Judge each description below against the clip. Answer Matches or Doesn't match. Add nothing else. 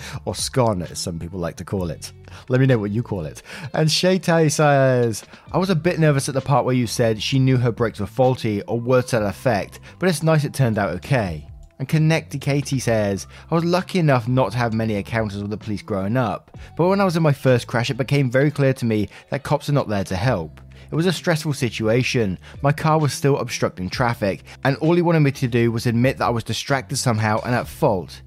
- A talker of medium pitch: Doesn't match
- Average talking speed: Doesn't match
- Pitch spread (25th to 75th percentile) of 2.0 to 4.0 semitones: Doesn't match